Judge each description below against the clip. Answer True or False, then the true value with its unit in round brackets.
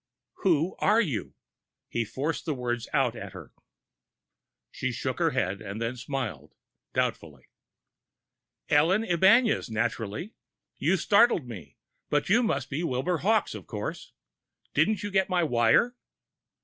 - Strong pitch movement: True (8.5 semitones)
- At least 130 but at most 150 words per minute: True (135 wpm)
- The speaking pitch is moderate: True (145 Hz)